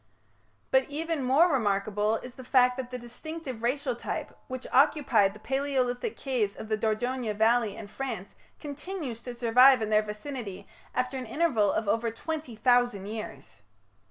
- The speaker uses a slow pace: No, average, 155 wpm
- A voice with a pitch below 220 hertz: No, high, 245 Hz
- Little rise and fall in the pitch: No, average, 3.7 semitones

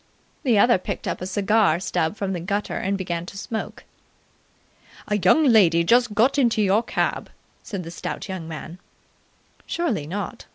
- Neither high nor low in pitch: No, high, 200 Hz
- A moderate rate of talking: Yes, average, 165 wpm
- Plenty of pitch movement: No, average, 3.8 semitones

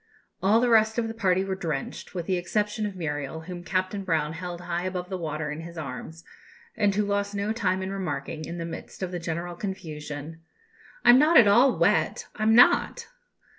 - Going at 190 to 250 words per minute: Yes, average, 200 wpm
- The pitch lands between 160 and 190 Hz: Yes, medium, 185 Hz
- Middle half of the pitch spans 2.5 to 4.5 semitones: Yes, average, 3.8 semitones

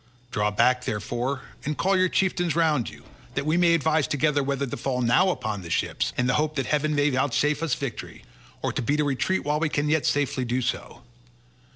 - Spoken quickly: Yes, fast, 215 wpm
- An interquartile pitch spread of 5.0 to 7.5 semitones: No, average, 3.4 semitones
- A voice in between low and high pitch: Yes, medium, 145 Hz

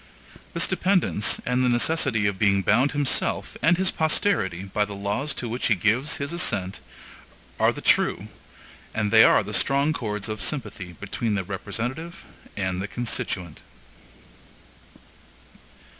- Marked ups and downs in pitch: Yes, wide, 5.9 semitones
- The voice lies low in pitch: Yes, low, 110 Hz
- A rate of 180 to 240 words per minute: No, average, 145 wpm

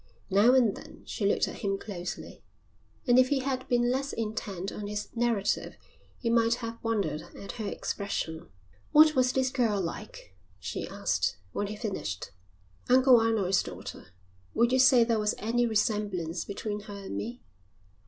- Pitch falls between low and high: No, high, 220 Hz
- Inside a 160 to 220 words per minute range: Yes, average, 165 wpm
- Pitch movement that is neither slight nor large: Yes, average, 3.5 semitones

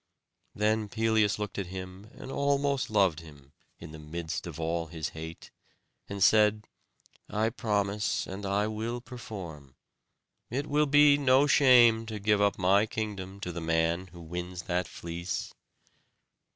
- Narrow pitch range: No, average, 4.5 semitones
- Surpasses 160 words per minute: No, average, 150 wpm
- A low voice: Yes, low, 100 Hz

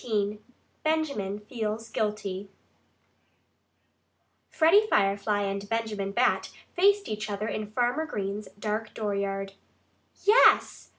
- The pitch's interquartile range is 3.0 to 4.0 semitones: Yes, average, 3.3 semitones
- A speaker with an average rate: No, slow, 100 wpm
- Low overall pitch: No, high, 210 Hz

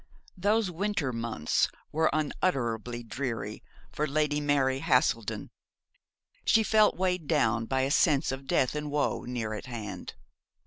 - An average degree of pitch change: Yes, average, 4.9 semitones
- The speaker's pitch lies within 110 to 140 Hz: Yes, low, 135 Hz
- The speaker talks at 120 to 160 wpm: Yes, slow, 135 wpm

